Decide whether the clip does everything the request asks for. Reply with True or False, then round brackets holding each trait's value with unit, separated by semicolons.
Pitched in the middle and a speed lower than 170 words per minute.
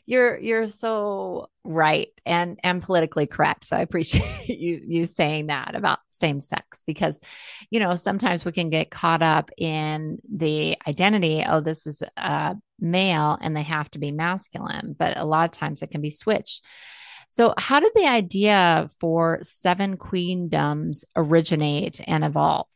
True (170 Hz; 160 wpm)